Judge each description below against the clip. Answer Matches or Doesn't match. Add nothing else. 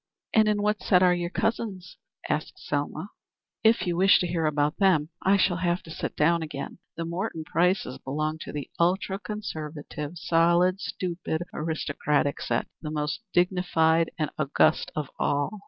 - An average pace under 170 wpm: Matches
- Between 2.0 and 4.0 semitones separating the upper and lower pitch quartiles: Matches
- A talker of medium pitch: Matches